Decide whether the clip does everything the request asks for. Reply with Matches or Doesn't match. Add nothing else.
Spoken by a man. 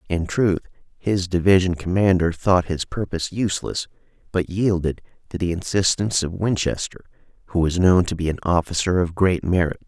Matches